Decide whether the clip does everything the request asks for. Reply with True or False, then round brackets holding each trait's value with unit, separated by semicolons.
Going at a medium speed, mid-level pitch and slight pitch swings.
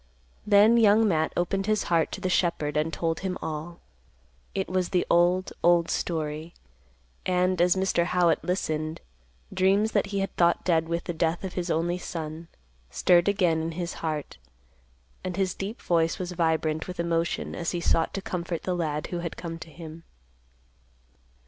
True (175 wpm; 175 Hz; 2.2 semitones)